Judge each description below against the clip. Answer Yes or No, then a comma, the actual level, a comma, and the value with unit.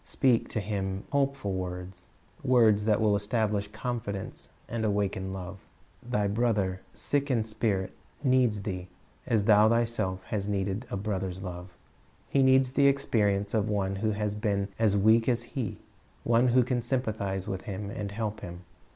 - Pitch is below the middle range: Yes, low, 105 Hz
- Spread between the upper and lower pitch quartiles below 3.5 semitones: Yes, average, 3.0 semitones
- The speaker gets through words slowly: No, average, 165 wpm